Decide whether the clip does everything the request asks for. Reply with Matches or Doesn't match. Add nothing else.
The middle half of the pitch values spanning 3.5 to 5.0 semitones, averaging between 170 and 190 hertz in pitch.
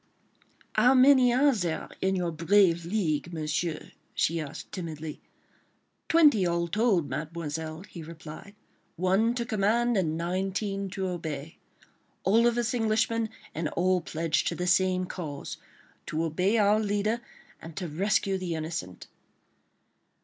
Matches